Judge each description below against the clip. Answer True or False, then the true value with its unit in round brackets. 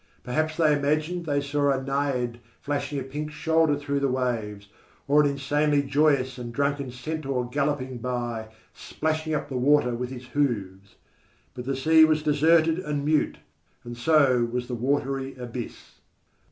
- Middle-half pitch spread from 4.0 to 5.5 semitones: False (3.1 semitones)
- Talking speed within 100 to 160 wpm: True (155 wpm)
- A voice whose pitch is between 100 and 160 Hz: True (140 Hz)